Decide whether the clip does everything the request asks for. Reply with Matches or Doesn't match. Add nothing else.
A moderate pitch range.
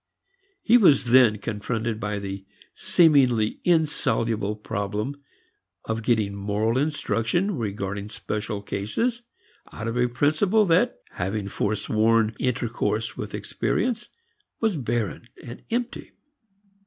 Doesn't match